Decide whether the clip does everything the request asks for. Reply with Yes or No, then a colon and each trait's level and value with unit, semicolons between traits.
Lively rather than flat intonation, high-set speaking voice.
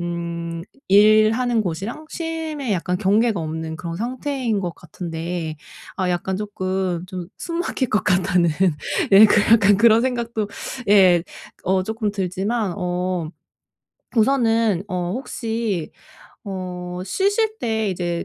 No: average, 4.3 semitones; high, 195 Hz